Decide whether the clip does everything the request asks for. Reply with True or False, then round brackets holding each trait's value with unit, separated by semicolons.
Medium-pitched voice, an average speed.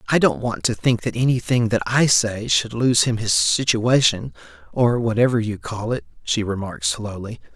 False (115 Hz; 175 wpm)